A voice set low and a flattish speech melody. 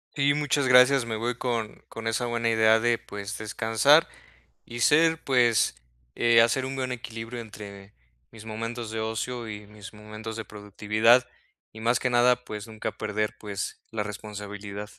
Yes: low, 115 Hz; narrow, 2.3 semitones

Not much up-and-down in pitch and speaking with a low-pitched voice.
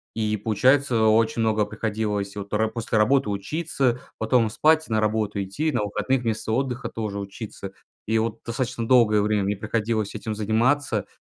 Yes: narrow, 2.3 semitones; low, 110 Hz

